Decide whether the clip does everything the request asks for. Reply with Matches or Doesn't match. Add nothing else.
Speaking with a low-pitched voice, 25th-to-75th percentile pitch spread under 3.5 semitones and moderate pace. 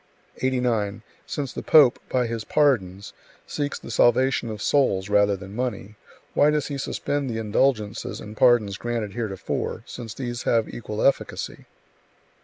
Doesn't match